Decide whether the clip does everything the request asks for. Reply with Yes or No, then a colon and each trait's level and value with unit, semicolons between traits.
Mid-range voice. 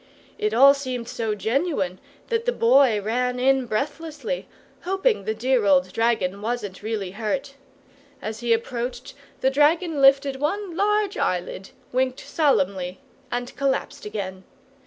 No: very high, 250 Hz